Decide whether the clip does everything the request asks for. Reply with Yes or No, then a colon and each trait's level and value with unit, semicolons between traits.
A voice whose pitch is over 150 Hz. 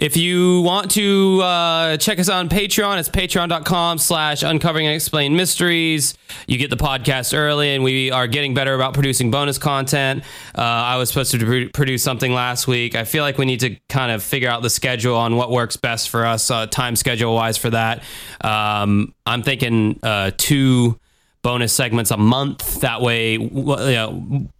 No: low, 135 Hz